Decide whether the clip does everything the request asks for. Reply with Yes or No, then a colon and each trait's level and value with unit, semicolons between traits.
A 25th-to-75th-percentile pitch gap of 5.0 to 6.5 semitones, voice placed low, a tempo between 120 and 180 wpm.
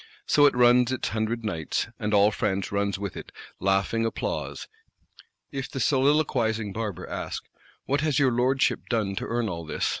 No: average, 4.5 semitones; low, 115 Hz; average, 170 wpm